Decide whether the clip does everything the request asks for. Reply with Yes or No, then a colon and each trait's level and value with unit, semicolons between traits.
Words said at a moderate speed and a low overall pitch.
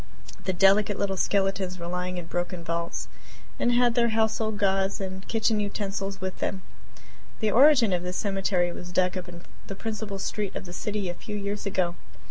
No: average, 185 wpm; high, 195 Hz